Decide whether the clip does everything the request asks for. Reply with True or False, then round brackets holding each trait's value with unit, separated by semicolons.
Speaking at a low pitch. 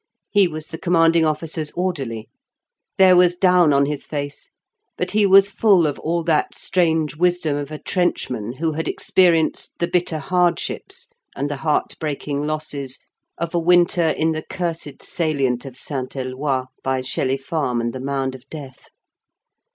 False (155 Hz)